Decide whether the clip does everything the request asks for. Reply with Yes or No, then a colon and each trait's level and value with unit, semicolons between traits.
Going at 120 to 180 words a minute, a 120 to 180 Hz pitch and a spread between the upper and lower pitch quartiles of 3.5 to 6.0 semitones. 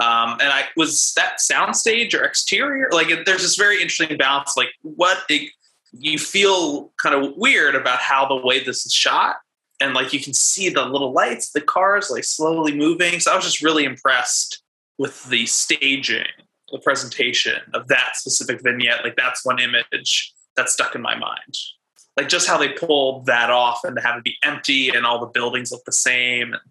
No: average, 195 wpm; medium, 140 Hz; average, 4.7 semitones